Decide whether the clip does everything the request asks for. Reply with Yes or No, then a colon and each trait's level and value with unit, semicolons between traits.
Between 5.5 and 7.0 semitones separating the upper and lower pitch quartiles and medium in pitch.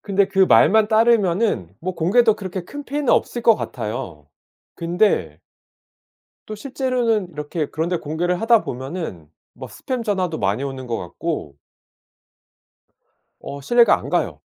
No: wide, 8.0 semitones; medium, 180 Hz